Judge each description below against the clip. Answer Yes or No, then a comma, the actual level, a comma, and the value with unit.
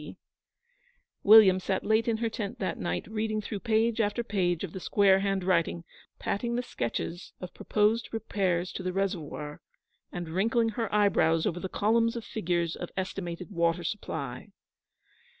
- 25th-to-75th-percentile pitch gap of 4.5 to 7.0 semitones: No, average, 3.8 semitones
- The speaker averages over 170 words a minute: No, average, 155 wpm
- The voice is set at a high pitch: Yes, high, 195 Hz